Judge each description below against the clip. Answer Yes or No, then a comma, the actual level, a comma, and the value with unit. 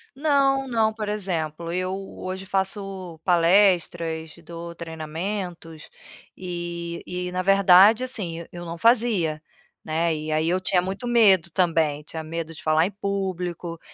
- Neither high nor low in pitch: Yes, medium, 180 Hz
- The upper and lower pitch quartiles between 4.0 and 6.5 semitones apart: No, average, 3.0 semitones